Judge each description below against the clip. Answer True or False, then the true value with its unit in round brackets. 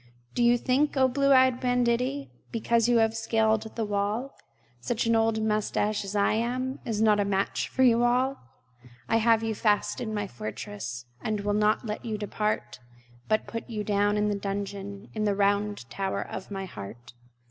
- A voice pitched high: True (215 Hz)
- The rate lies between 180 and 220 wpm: True (185 wpm)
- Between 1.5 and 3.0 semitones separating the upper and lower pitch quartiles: True (2.7 semitones)